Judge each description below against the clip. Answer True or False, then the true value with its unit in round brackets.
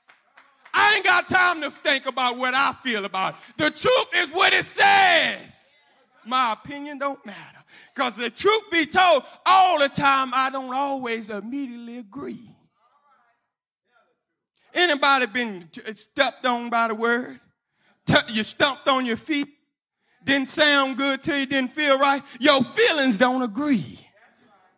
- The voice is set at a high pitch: True (275 Hz)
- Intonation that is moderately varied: True (4.0 semitones)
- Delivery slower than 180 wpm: True (150 wpm)